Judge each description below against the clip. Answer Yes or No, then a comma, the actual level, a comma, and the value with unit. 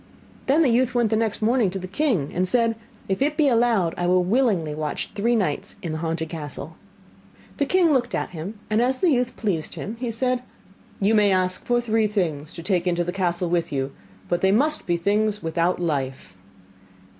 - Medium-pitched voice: No, high, 200 Hz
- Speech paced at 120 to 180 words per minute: No, average, 200 wpm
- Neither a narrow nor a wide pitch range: No, wide, 5.7 semitones